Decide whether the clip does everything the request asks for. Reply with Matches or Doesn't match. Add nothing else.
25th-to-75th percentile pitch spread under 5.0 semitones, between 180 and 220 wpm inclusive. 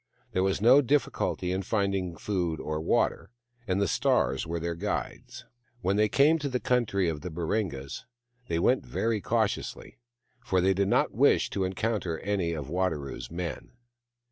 Doesn't match